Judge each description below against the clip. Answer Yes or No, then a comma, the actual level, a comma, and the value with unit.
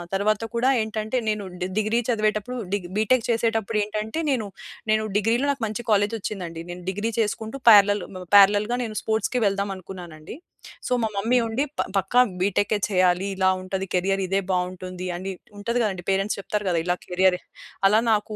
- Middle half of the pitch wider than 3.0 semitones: No, average, 2.7 semitones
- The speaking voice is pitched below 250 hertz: Yes, high, 205 Hz